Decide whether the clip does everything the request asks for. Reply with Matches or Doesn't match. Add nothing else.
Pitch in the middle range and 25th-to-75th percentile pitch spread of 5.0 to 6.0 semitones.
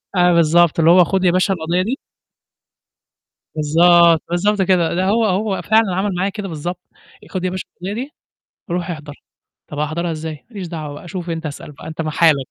Doesn't match